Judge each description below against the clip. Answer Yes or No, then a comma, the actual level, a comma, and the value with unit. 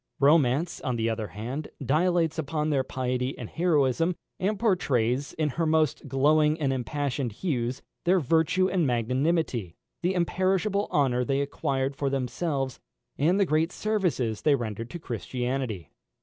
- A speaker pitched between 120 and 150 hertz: Yes, medium, 140 Hz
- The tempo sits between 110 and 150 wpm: Yes, average, 145 wpm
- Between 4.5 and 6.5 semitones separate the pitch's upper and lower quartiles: Yes, average, 4.8 semitones